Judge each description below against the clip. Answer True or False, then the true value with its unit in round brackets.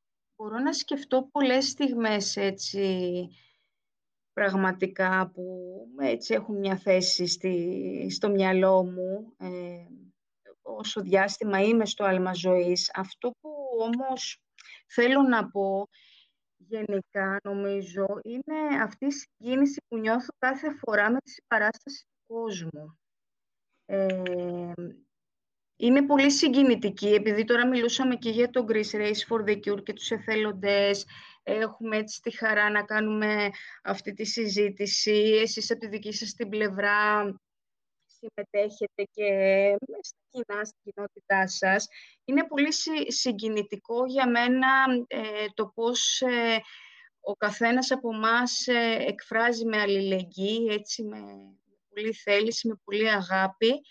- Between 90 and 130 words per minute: True (120 wpm)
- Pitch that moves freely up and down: False (3.3 semitones)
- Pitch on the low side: False (215 Hz)